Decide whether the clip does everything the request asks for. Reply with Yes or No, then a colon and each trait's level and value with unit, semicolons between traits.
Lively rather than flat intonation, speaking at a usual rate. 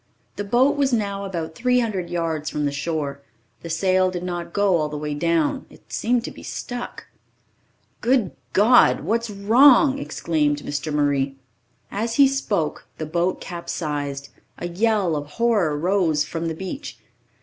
Yes: wide, 6.6 semitones; average, 160 wpm